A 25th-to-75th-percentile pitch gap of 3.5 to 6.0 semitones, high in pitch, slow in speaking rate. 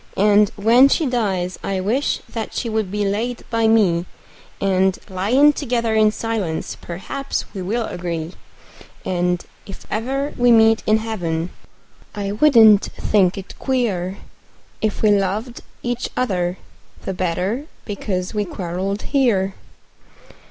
Yes: average, 3.8 semitones; high, 210 Hz; slow, 130 wpm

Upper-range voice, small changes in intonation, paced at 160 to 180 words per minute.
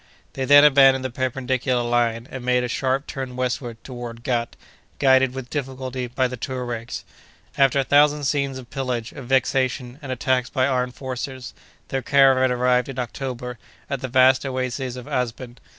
No: low, 130 Hz; narrow, 1.4 semitones; average, 165 wpm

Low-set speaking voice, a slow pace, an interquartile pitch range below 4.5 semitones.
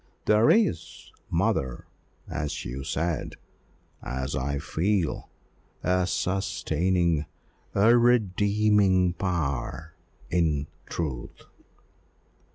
No: very low, 85 Hz; slow, 75 wpm; wide, 5.4 semitones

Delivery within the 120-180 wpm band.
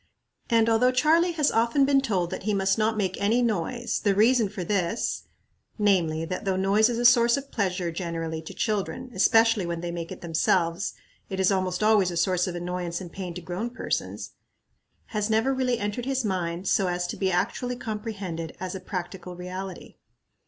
No: average, 190 wpm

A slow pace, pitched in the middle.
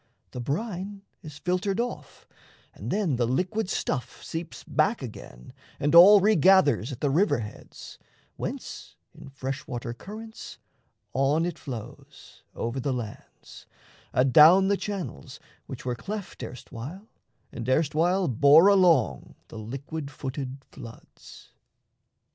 Yes: slow, 125 wpm; medium, 150 Hz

